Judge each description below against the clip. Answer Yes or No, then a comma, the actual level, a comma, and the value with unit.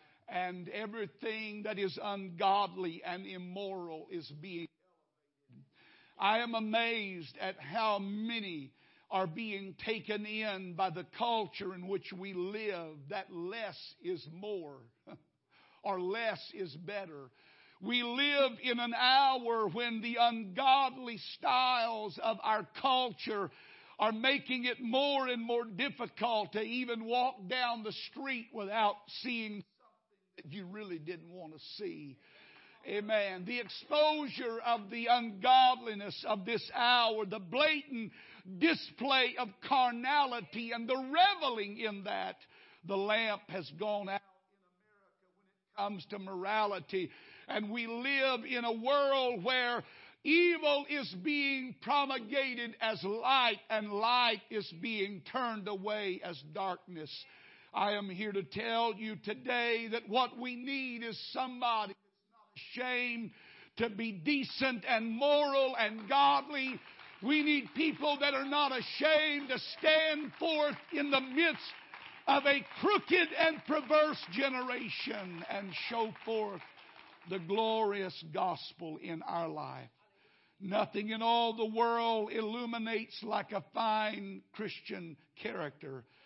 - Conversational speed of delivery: No, slow, 125 wpm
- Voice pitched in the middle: No, high, 220 Hz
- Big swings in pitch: No, average, 4.6 semitones